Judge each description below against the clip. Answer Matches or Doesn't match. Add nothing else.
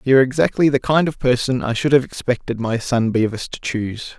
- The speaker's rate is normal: Doesn't match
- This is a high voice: Doesn't match